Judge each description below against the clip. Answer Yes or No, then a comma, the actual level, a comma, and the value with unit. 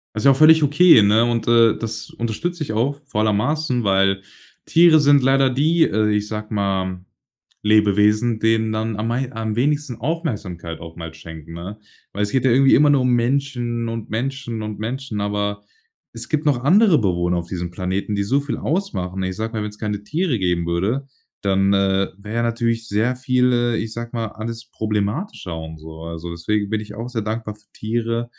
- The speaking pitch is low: Yes, low, 110 Hz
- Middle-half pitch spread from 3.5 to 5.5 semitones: Yes, average, 3.9 semitones